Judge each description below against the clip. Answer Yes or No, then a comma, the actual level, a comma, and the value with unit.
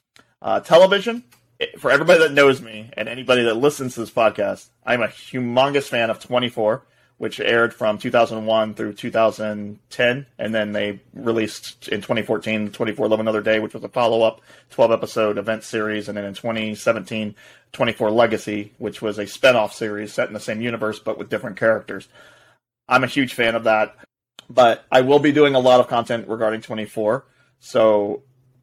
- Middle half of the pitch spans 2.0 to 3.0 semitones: Yes, narrow, 2.4 semitones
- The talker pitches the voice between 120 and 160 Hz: No, low, 110 Hz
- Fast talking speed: No, average, 170 wpm